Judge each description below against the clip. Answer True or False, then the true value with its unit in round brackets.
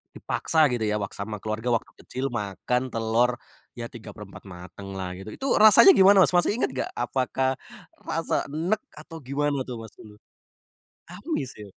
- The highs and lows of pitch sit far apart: True (6.0 semitones)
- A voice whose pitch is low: True (125 Hz)